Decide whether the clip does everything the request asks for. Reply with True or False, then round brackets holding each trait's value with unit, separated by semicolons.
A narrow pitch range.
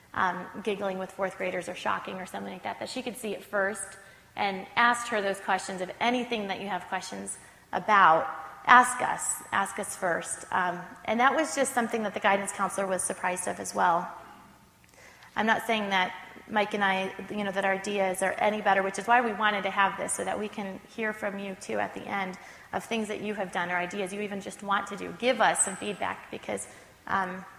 True (2.0 semitones)